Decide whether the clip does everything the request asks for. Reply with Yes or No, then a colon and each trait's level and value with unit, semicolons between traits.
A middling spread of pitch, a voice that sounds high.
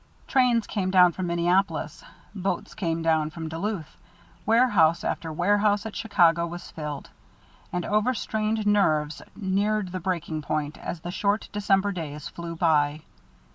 No: average, 4.2 semitones; medium, 180 Hz